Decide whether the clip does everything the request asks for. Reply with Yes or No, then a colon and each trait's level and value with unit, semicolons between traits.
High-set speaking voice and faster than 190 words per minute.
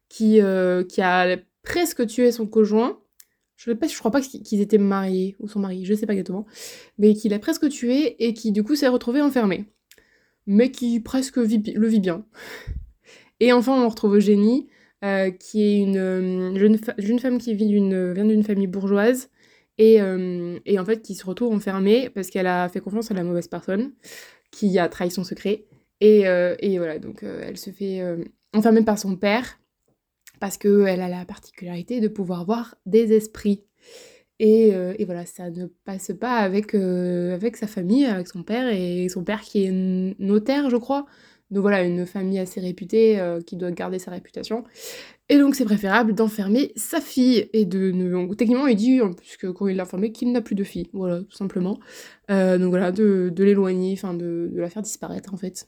Yes: high, 205 Hz; average, 200 wpm